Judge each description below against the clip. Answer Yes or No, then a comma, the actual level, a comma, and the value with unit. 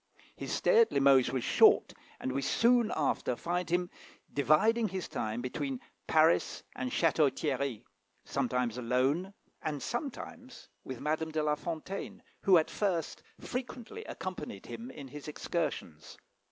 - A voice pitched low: No, medium, 155 Hz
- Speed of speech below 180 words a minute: Yes, average, 140 wpm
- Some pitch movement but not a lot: No, wide, 6.2 semitones